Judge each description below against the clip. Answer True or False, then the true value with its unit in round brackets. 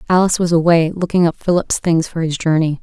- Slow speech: False (215 wpm)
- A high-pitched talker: False (165 Hz)